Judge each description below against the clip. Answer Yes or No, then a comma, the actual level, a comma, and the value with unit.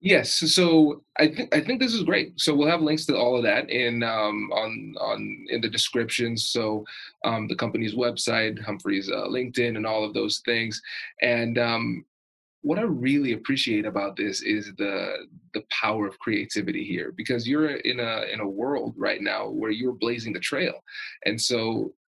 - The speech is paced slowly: No, average, 185 wpm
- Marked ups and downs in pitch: Yes, wide, 5.7 semitones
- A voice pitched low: Yes, low, 120 Hz